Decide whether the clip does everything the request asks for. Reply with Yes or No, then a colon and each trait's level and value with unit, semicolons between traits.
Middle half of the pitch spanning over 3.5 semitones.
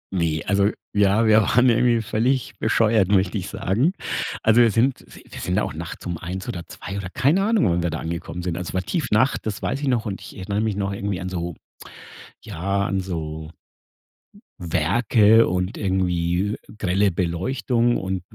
Yes: average, 4.1 semitones